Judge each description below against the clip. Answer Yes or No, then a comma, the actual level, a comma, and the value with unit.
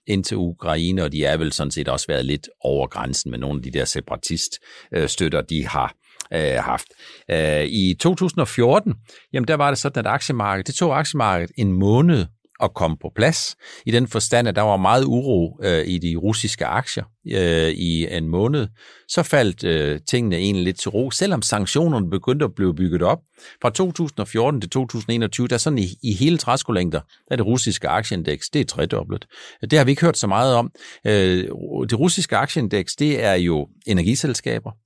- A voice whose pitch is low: Yes, low, 110 Hz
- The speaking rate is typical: Yes, average, 190 wpm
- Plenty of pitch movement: Yes, wide, 6.6 semitones